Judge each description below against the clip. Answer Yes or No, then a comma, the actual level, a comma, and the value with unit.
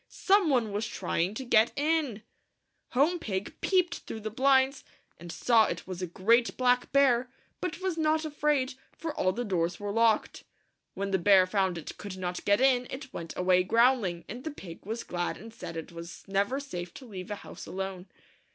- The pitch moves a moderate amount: No, wide, 6.2 semitones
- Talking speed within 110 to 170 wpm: No, average, 195 wpm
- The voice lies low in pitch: No, high, 220 Hz